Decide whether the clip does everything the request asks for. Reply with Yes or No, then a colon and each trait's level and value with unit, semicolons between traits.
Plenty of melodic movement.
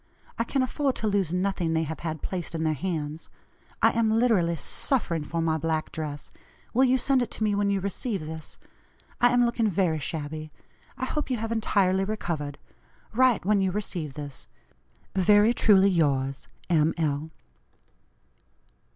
Yes: wide, 5.7 semitones